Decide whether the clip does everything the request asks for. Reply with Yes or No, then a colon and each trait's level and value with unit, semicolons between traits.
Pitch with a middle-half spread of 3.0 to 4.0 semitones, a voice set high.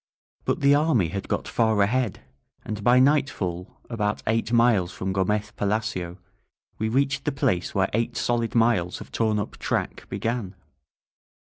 No: average, 3.6 semitones; low, 110 Hz